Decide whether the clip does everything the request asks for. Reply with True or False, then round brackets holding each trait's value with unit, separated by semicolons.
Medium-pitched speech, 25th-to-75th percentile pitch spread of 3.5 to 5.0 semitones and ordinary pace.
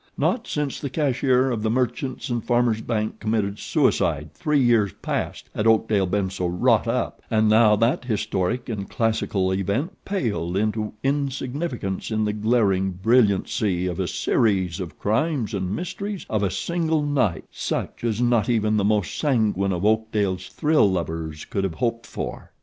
False (110 Hz; 4.2 semitones; 160 wpm)